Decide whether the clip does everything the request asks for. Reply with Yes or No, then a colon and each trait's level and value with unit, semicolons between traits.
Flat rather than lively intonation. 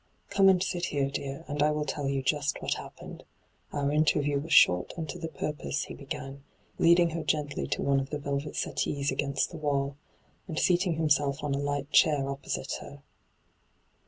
Yes: narrow, 2.0 semitones